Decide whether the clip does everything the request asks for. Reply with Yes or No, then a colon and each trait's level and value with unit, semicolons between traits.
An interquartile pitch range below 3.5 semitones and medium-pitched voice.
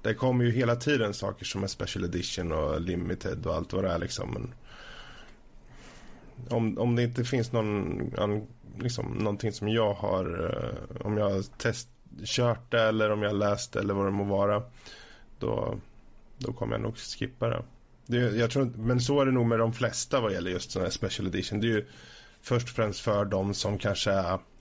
No: average, 3.0 semitones; low, 115 Hz